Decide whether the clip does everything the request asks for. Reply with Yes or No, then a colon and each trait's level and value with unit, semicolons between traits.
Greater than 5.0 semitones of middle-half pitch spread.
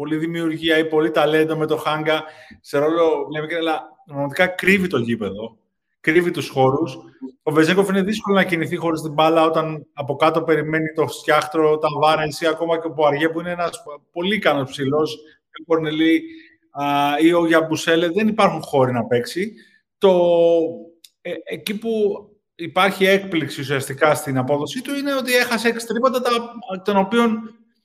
No: average, 4.1 semitones